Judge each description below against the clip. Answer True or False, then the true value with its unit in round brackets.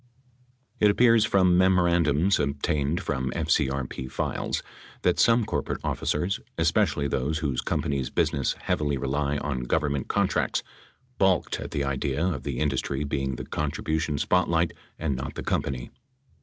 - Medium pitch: False (75 Hz)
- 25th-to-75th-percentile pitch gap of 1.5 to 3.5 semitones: False (4.2 semitones)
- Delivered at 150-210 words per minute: False (140 wpm)